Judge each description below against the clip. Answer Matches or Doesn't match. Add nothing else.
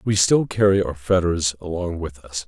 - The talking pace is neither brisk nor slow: Matches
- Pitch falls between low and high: Doesn't match